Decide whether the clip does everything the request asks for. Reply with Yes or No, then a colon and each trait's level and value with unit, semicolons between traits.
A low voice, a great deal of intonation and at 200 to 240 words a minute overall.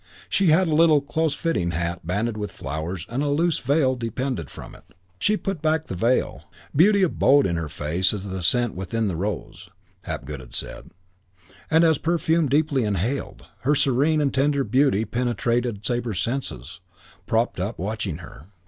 No: low, 120 Hz; wide, 7.7 semitones; average, 165 wpm